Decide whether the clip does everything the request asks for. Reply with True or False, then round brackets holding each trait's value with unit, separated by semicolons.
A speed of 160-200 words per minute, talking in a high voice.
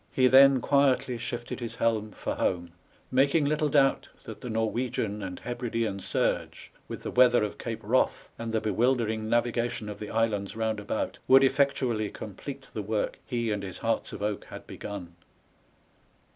False (165 wpm; 115 Hz)